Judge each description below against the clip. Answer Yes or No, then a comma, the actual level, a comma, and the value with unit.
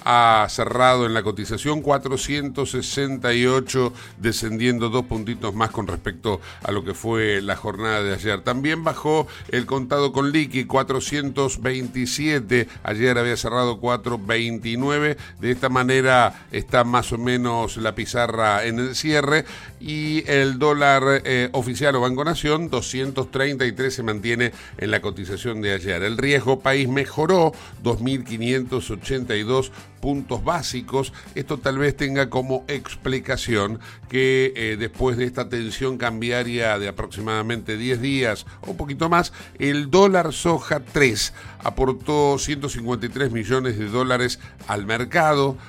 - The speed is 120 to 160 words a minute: Yes, average, 130 wpm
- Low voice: Yes, low, 125 Hz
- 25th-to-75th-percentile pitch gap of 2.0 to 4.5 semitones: Yes, average, 3.3 semitones